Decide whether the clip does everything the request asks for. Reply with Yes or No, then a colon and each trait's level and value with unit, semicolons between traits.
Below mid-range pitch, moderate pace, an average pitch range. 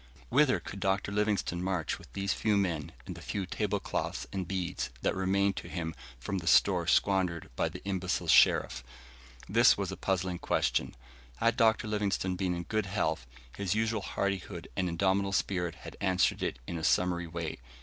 No: very low, 95 Hz; average, 180 wpm; narrow, 2.3 semitones